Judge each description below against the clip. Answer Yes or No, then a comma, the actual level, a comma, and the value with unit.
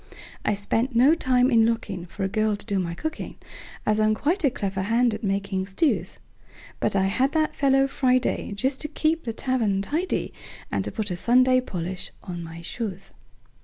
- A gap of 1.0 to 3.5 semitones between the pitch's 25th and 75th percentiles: No, average, 5.0 semitones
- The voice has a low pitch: No, high, 225 Hz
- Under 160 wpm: No, average, 165 wpm